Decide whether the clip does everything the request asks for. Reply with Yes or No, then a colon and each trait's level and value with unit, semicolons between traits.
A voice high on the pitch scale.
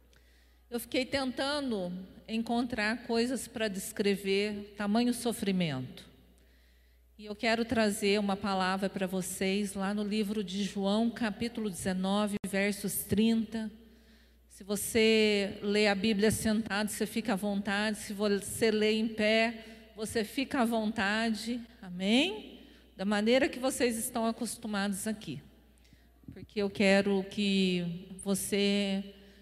Yes: high, 210 Hz